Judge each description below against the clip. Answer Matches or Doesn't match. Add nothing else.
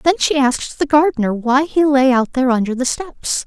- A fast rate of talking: Matches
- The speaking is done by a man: Doesn't match